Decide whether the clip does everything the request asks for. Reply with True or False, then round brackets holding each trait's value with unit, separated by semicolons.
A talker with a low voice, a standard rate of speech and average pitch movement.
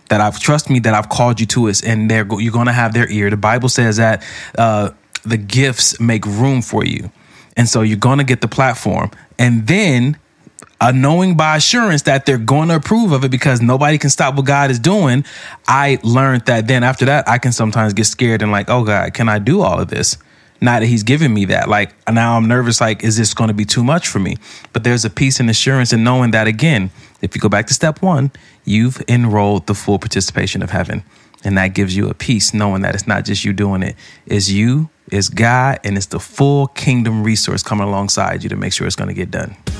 False (115 Hz; 240 wpm; 4.0 semitones)